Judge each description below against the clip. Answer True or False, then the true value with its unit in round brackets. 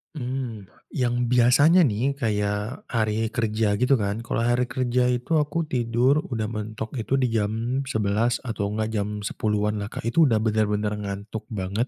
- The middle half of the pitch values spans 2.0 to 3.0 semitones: True (2.6 semitones)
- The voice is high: False (110 Hz)